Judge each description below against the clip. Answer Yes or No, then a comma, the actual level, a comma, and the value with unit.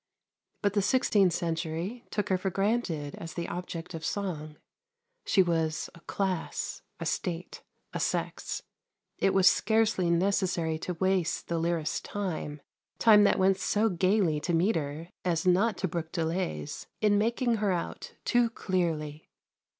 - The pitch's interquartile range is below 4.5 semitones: Yes, average, 3.6 semitones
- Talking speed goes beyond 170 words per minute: No, average, 145 wpm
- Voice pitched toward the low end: No, medium, 180 Hz